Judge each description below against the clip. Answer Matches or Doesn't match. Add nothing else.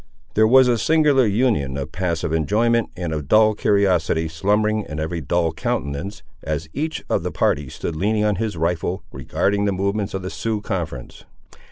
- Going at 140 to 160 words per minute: Doesn't match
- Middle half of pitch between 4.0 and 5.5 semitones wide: Matches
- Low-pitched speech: Matches